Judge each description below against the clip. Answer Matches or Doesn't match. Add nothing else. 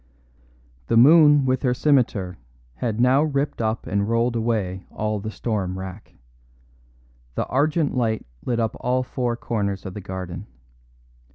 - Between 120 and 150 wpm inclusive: Matches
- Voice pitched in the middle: Doesn't match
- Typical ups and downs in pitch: Matches